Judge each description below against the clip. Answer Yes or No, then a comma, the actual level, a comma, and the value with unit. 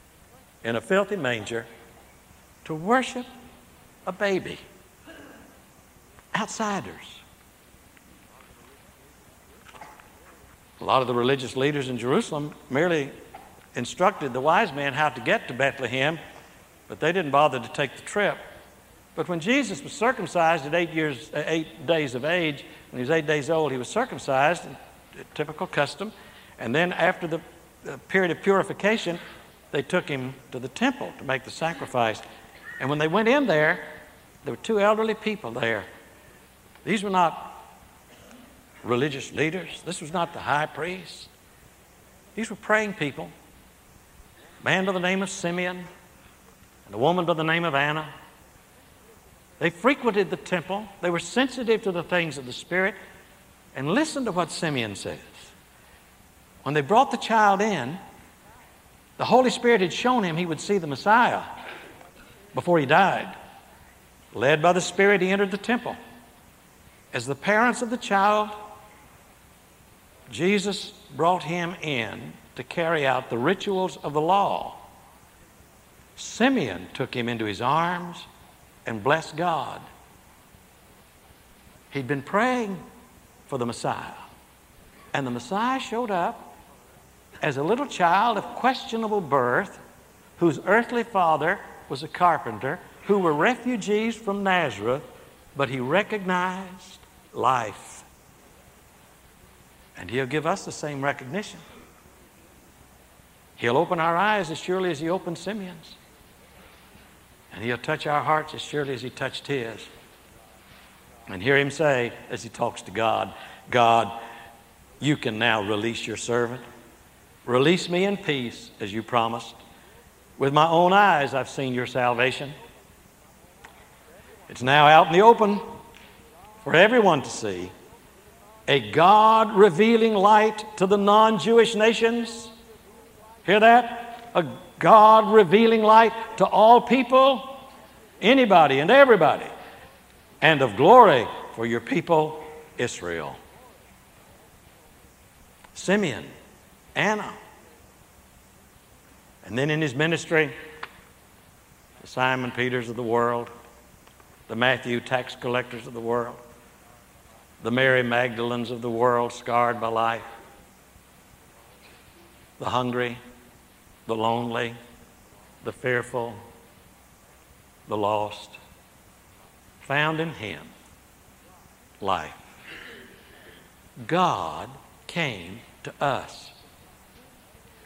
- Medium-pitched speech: Yes, medium, 155 Hz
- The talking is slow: Yes, slow, 125 wpm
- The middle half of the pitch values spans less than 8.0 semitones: No, wide, 8.7 semitones